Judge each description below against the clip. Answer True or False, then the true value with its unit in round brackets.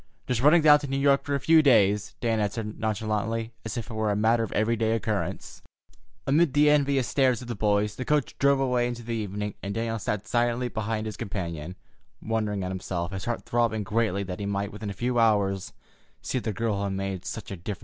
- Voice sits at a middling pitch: False (110 Hz)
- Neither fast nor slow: False (235 wpm)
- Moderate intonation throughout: True (3.1 semitones)